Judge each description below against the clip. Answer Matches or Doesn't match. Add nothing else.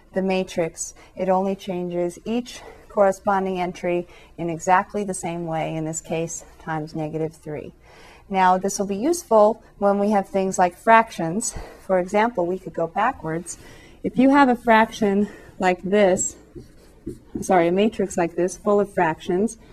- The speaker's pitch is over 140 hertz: Matches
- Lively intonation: Doesn't match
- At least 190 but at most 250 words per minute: Doesn't match